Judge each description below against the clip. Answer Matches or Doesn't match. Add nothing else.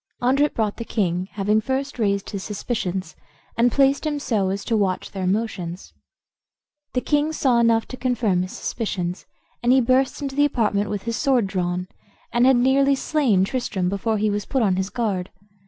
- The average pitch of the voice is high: Matches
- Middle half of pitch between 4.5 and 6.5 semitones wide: Matches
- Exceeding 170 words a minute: Matches